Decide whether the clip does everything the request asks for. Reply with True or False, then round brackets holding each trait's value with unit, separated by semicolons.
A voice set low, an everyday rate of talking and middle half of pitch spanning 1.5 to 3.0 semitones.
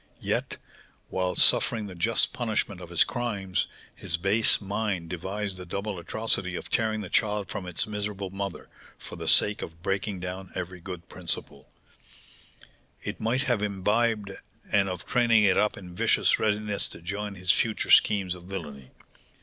True (100 Hz; 160 wpm; 2.6 semitones)